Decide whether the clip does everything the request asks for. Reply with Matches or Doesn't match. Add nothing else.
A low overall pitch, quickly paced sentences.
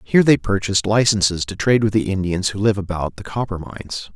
Matches